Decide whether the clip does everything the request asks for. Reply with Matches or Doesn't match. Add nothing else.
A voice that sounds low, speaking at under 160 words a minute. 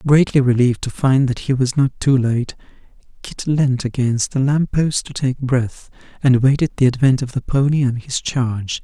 Doesn't match